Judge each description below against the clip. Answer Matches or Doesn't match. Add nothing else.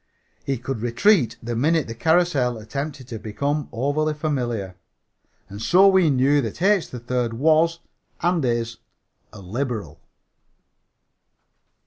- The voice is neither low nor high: Doesn't match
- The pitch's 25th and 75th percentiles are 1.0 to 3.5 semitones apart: Doesn't match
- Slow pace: Matches